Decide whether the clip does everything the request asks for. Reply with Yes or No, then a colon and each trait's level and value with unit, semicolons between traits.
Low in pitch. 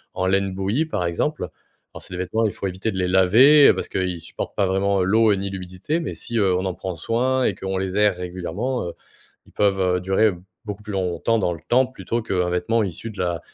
Yes: very low, 95 Hz